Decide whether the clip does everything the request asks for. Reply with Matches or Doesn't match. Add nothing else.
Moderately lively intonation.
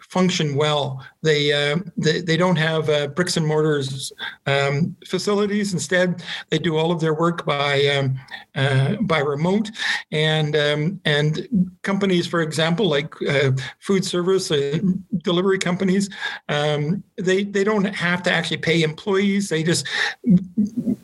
Matches